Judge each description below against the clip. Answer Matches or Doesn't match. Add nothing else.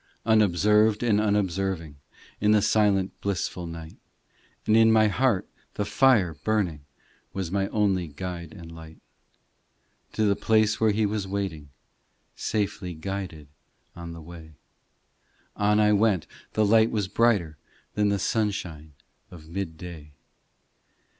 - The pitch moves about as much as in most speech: Matches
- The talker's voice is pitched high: Doesn't match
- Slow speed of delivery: Matches